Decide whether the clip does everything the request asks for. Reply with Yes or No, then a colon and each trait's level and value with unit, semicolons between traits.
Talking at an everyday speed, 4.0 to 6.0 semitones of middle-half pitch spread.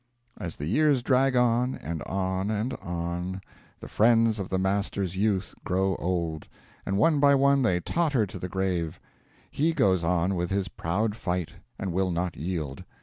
Yes: average, 170 wpm; average, 4.6 semitones